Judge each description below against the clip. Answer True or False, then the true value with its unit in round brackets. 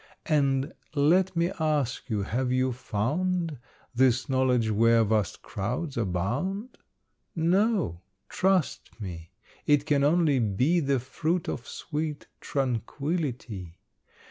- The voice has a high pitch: False (135 Hz)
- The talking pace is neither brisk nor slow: False (110 wpm)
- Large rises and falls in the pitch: True (5.7 semitones)